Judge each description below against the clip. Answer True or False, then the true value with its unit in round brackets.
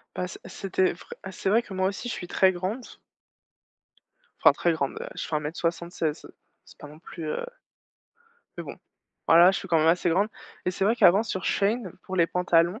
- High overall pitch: False (180 Hz)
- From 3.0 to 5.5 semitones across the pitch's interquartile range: False (2.6 semitones)